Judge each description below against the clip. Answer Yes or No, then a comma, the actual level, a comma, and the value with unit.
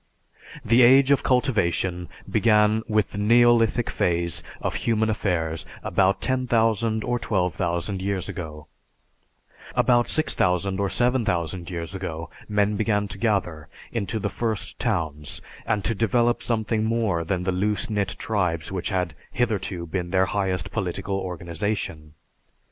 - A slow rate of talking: Yes, slow, 130 wpm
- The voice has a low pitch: Yes, low, 100 Hz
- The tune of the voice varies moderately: Yes, average, 4.2 semitones